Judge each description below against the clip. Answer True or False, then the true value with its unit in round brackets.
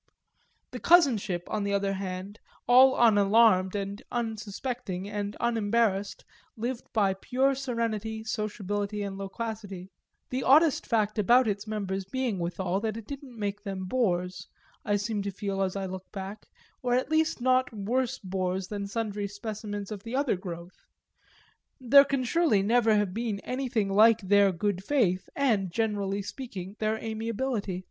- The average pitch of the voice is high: True (210 Hz)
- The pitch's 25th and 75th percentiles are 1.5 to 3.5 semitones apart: True (3.2 semitones)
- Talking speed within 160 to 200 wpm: False (150 wpm)